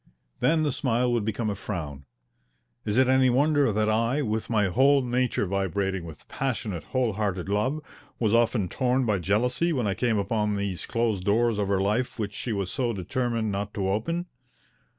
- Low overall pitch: Yes, low, 110 Hz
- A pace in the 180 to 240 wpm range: Yes, average, 185 wpm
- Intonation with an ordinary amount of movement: Yes, average, 3.9 semitones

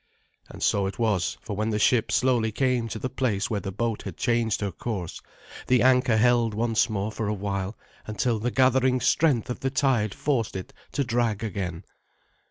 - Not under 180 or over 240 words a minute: Yes, average, 190 wpm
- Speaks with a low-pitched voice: Yes, low, 115 Hz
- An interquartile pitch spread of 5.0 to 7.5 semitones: No, average, 3.3 semitones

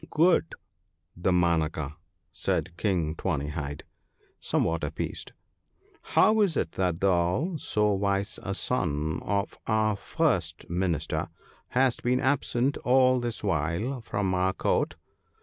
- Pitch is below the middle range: Yes, very low, 95 Hz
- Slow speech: Yes, slow, 125 wpm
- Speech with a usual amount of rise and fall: No, wide, 6.8 semitones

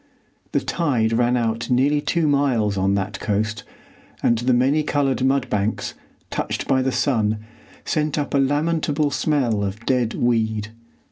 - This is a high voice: No, low, 125 Hz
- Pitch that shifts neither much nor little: Yes, average, 4.5 semitones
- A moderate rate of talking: Yes, average, 150 wpm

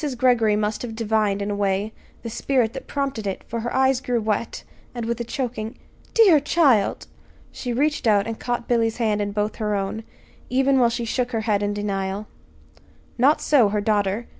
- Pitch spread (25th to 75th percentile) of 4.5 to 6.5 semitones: No, average, 3.0 semitones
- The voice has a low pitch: No, high, 225 Hz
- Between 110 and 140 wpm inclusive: No, average, 190 wpm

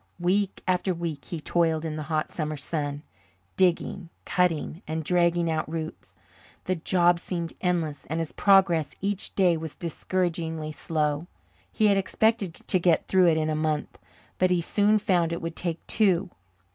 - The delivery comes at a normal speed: Yes, average, 160 wpm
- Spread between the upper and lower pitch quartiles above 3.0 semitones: No, average, 2.7 semitones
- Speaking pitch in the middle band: Yes, medium, 170 Hz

